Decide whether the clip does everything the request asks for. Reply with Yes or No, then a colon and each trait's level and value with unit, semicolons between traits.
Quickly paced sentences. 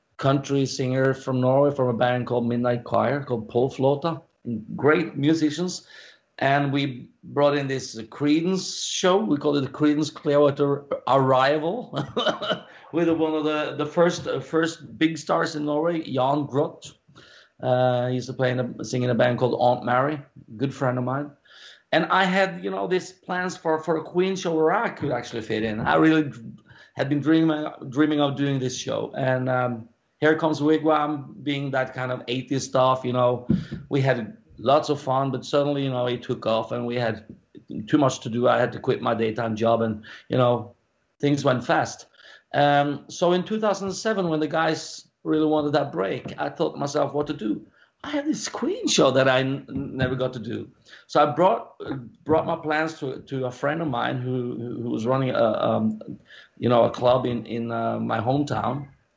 No: average, 195 wpm